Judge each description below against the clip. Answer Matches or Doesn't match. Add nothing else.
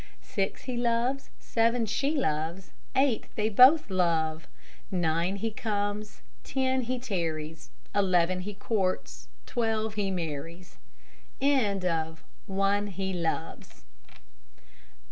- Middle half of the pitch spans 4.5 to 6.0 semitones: Matches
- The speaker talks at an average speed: Doesn't match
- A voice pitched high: Matches